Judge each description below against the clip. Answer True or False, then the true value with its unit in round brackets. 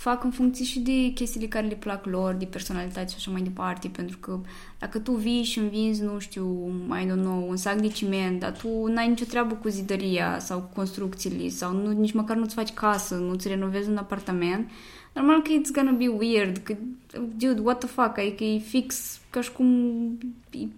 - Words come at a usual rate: False (205 wpm)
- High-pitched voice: True (215 Hz)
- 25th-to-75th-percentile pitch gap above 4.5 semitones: False (4.2 semitones)